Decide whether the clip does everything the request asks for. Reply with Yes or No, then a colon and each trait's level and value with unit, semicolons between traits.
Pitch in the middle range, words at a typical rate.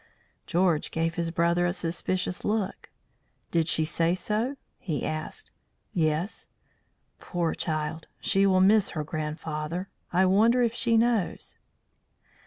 No: medium, 175 Hz; slow, 125 wpm